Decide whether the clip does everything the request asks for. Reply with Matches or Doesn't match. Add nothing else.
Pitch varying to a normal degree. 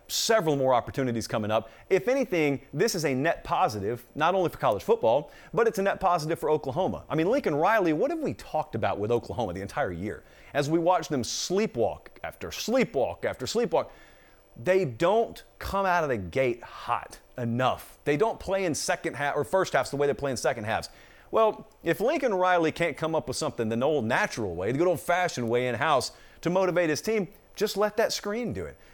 Doesn't match